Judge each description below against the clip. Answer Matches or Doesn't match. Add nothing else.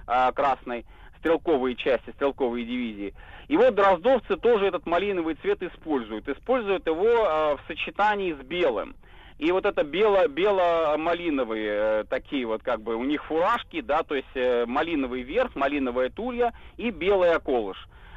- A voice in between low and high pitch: Matches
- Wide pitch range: Matches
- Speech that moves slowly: Doesn't match